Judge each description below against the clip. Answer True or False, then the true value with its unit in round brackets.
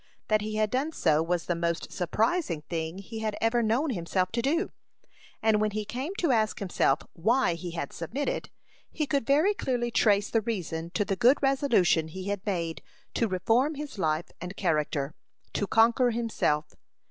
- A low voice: False (215 Hz)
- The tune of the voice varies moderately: False (6.0 semitones)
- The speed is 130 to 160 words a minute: False (180 wpm)